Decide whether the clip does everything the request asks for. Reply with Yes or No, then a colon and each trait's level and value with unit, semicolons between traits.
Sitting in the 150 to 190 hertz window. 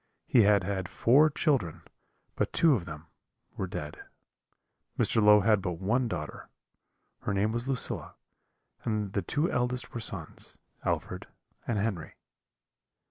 No: low, 105 Hz